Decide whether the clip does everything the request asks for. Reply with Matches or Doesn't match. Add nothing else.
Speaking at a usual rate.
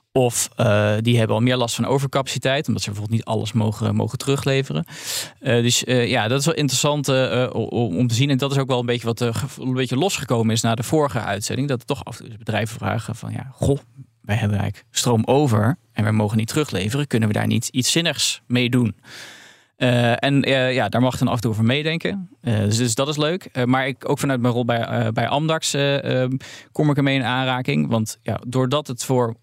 Doesn't match